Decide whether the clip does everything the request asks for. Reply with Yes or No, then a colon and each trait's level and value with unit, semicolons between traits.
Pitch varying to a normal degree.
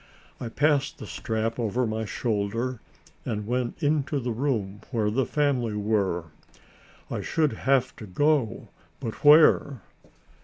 Yes: average, 4.3 semitones